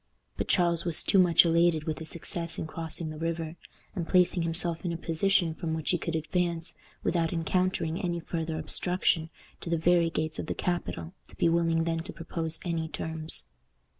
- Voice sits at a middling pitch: Yes, medium, 165 Hz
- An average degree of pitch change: No, narrow, 1.3 semitones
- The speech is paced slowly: No, average, 190 wpm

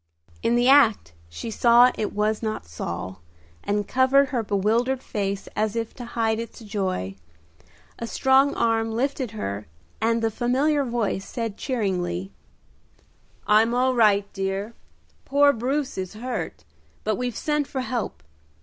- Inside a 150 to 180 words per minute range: No, average, 140 wpm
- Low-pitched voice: No, high, 225 Hz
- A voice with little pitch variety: No, average, 3.8 semitones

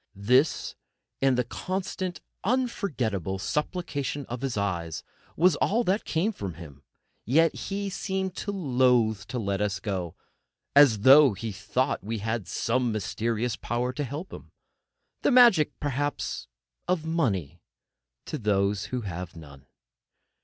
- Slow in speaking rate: Yes, slow, 130 wpm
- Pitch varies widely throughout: Yes, wide, 8.0 semitones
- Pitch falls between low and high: No, low, 125 Hz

